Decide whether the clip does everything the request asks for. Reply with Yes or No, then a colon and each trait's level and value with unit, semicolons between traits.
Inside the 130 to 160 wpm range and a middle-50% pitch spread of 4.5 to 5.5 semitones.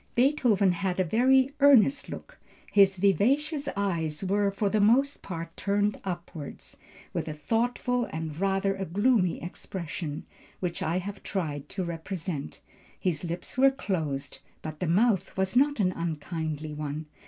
Yes: average, 145 wpm; average, 4.9 semitones